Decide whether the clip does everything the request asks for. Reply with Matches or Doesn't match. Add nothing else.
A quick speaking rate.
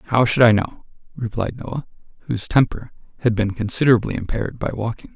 Doesn't match